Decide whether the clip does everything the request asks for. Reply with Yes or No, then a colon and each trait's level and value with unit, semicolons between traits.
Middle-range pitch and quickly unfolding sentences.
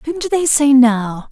No: very high, 270 Hz; fast, 230 wpm